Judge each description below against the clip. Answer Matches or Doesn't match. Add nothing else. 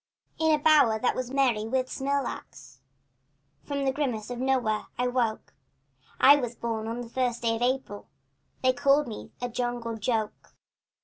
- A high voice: Matches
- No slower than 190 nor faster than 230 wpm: Doesn't match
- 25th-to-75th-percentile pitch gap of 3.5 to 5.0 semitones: Doesn't match